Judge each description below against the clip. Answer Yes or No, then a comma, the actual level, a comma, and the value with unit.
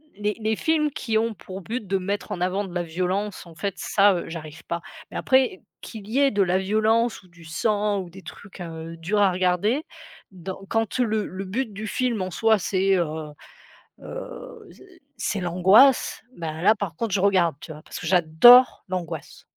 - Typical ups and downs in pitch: Yes, average, 3.5 semitones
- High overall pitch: Yes, high, 195 Hz